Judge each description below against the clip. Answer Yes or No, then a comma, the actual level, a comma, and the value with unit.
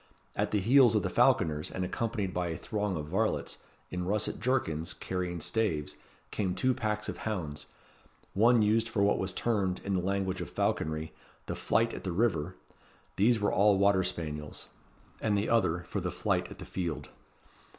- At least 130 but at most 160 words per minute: No, average, 180 wpm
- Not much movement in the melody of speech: No, average, 3.6 semitones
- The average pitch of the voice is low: Yes, very low, 95 Hz